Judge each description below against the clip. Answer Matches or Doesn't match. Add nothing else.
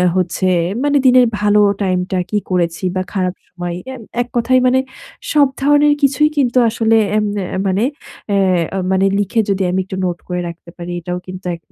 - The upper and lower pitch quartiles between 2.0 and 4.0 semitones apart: Doesn't match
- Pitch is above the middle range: Matches